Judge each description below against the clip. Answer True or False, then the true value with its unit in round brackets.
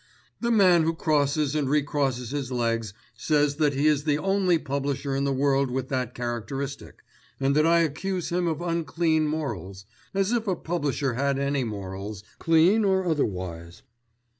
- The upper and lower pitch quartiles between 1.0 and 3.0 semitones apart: False (4.3 semitones)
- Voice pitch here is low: False (145 Hz)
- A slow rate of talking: False (165 wpm)